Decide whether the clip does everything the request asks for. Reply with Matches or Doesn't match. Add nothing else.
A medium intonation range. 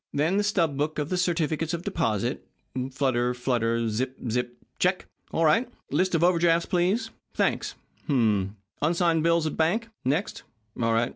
Doesn't match